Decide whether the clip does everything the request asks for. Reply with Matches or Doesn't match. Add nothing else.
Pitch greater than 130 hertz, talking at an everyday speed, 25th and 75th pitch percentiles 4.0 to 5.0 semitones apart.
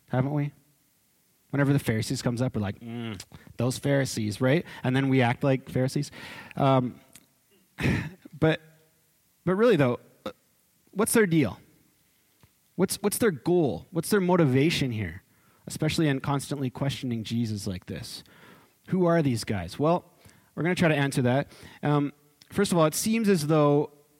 Matches